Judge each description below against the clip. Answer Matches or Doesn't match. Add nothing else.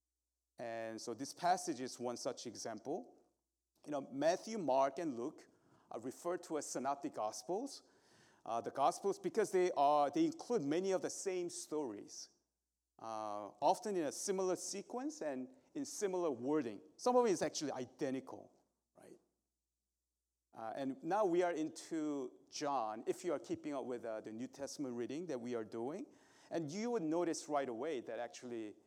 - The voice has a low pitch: Doesn't match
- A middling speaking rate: Matches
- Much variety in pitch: Matches